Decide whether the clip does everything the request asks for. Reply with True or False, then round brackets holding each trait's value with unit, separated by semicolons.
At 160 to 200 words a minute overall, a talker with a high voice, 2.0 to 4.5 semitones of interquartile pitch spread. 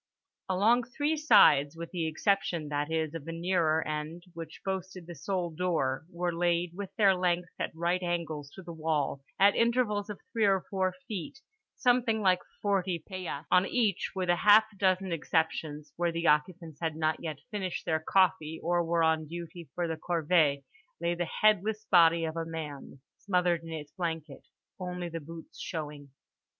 False (175 wpm; 170 Hz; 2.8 semitones)